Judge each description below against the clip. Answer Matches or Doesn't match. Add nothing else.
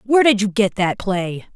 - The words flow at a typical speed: Doesn't match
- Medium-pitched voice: Doesn't match